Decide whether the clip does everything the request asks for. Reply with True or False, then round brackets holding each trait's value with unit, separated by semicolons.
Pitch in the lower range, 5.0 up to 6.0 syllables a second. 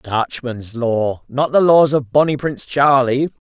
False (130 Hz; 4.0 syllables/s)